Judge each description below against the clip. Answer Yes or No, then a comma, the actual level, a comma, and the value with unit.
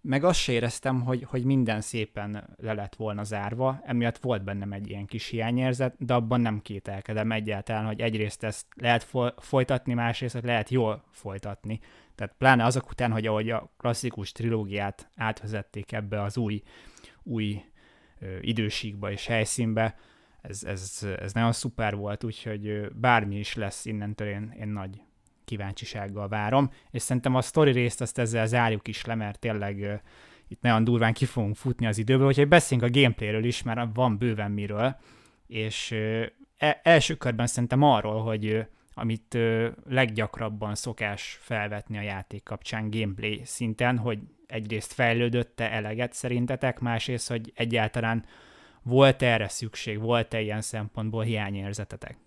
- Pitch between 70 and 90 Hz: No, low, 115 Hz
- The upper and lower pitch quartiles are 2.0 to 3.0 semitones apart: Yes, narrow, 2.5 semitones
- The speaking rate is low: No, average, 145 wpm